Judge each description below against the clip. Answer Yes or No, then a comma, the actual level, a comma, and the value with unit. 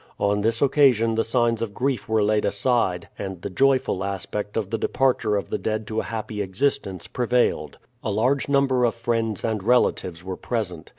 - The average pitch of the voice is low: Yes, low, 110 Hz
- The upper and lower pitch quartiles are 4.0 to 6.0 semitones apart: No, average, 3.5 semitones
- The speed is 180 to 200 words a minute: Yes, average, 185 wpm